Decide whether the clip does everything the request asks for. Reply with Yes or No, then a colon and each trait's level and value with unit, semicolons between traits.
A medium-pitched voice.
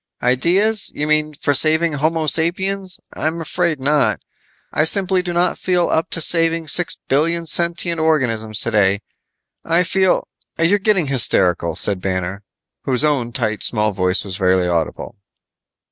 Yes: medium, 155 Hz